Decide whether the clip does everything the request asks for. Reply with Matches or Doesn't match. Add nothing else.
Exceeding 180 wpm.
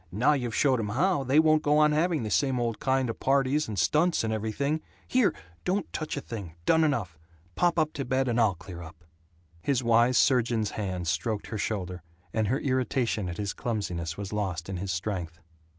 Matches